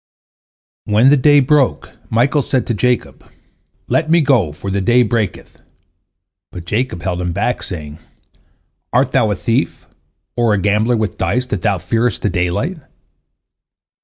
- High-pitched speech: No, low, 115 Hz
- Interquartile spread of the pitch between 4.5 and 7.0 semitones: Yes, average, 4.9 semitones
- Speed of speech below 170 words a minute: Yes, average, 150 wpm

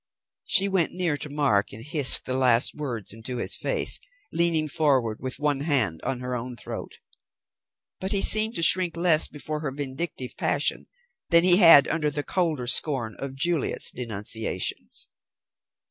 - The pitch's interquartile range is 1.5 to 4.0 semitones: No, average, 4.9 semitones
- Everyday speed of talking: Yes, average, 160 wpm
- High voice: No, medium, 145 Hz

